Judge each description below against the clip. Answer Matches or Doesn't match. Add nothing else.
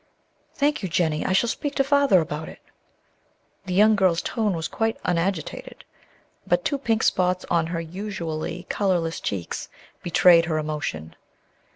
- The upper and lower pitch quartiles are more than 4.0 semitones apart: Matches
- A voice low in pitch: Doesn't match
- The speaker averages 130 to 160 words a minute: Matches